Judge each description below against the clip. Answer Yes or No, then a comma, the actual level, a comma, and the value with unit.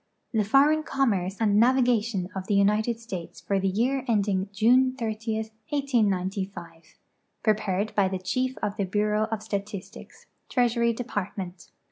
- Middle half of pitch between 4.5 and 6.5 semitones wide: No, average, 3.4 semitones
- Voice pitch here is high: Yes, high, 215 Hz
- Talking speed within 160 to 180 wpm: No, slow, 135 wpm